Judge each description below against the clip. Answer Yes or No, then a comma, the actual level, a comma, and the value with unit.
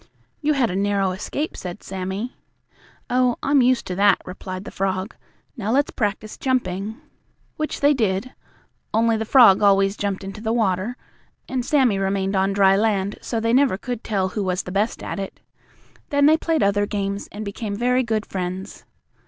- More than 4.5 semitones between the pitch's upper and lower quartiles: No, average, 4.0 semitones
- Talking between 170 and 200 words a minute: Yes, average, 175 wpm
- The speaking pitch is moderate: No, high, 205 Hz